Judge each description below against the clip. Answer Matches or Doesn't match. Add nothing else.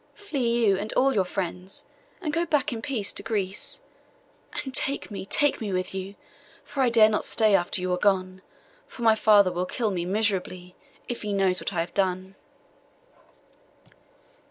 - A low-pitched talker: Doesn't match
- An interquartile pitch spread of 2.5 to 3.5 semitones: Doesn't match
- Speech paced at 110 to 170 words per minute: Doesn't match